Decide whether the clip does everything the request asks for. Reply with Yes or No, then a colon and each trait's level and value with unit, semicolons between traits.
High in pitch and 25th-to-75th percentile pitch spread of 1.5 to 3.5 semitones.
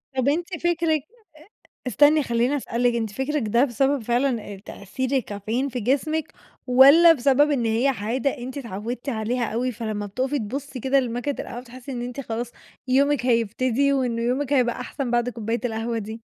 Yes: very high, 250 Hz; average, 3.1 semitones